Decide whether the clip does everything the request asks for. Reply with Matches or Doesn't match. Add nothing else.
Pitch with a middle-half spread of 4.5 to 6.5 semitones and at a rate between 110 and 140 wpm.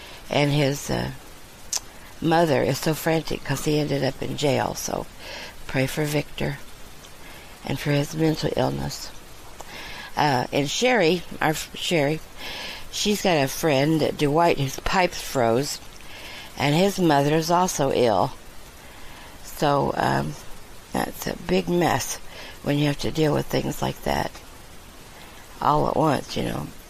Doesn't match